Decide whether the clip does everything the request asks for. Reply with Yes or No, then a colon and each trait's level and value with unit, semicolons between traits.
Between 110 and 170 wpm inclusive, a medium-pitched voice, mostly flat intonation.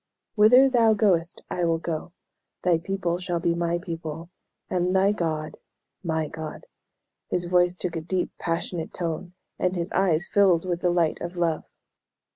Yes: average, 160 wpm; medium, 175 Hz; narrow, 1.8 semitones